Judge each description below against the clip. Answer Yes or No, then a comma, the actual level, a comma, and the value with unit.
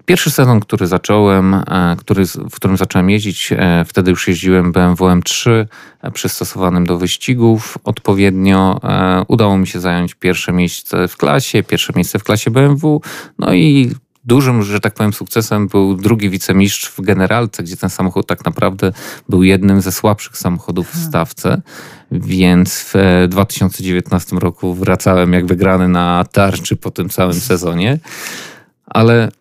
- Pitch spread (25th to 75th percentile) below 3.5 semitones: Yes, average, 2.9 semitones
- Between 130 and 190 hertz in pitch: No, very low, 95 Hz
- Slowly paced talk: No, average, 140 wpm